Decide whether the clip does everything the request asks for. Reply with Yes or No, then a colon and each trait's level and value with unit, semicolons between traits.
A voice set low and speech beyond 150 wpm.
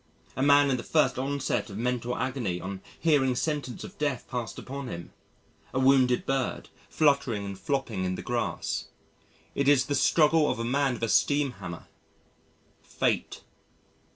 Yes: low, 130 Hz; average, 160 wpm